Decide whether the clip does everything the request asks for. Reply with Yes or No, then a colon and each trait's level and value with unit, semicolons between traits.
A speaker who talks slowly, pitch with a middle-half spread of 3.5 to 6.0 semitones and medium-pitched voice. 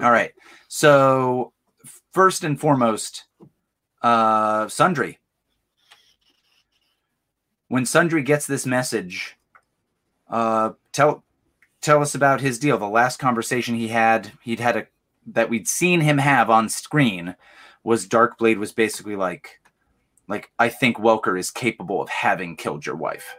No: slow, 130 wpm; average, 3.9 semitones; low, 120 Hz